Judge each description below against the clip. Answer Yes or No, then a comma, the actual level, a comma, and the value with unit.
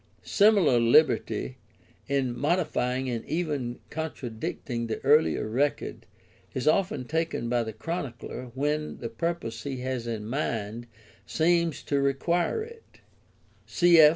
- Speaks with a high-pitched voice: No, low, 135 Hz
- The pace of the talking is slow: Yes, slow, 125 wpm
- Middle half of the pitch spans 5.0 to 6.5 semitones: Yes, average, 5.3 semitones